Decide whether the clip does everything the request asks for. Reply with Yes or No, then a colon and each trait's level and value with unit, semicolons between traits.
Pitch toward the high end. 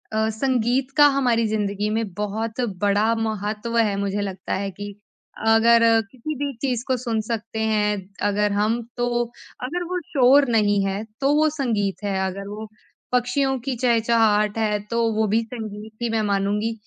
Yes: high, 220 Hz